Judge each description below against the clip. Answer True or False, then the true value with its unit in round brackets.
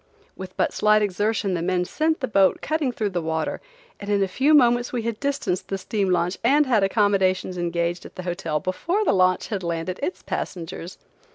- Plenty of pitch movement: False (4.5 semitones)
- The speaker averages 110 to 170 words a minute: False (200 wpm)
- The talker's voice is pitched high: True (195 Hz)